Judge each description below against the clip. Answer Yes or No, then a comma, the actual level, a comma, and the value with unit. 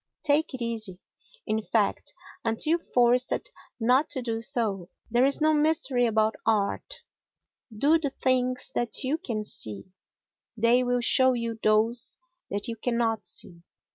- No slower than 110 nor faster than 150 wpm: Yes, average, 140 wpm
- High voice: Yes, high, 240 Hz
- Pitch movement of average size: Yes, average, 3.1 semitones